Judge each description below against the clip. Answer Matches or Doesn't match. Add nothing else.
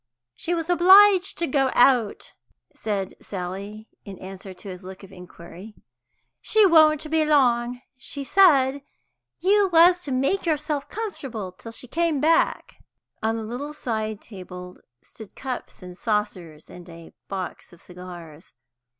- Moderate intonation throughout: Doesn't match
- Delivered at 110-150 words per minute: Matches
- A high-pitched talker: Matches